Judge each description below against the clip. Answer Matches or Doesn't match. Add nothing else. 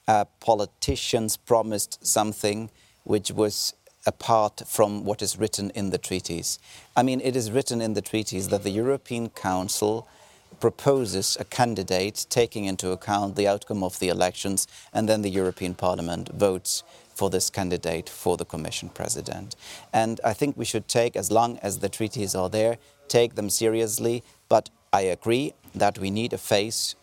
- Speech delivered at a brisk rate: Matches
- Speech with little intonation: Doesn't match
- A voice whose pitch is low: Matches